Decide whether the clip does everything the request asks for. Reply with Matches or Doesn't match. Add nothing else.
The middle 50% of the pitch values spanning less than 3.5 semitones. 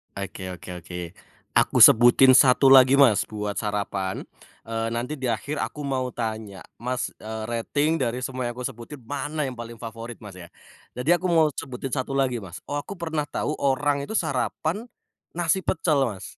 Doesn't match